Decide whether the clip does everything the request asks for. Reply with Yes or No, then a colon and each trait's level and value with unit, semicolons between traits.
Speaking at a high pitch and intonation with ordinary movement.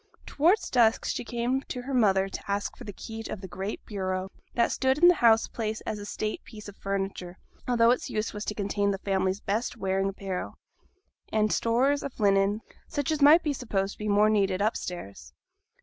Yes: high, 210 Hz; average, 3.6 semitones